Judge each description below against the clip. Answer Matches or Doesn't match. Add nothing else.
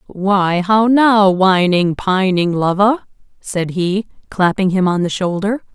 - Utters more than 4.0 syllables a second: Doesn't match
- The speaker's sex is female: Matches